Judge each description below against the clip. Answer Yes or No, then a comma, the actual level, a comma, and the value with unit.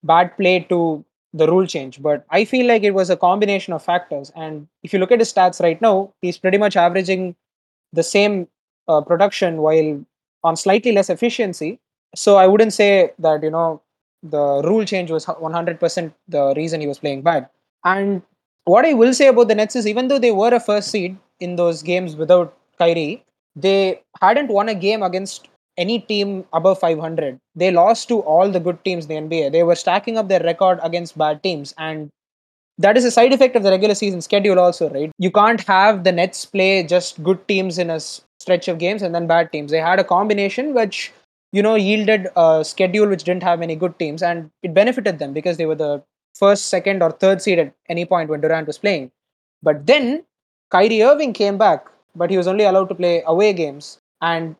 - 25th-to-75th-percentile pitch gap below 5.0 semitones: Yes, average, 3.7 semitones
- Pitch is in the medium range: Yes, medium, 180 Hz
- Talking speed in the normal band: No, fast, 210 wpm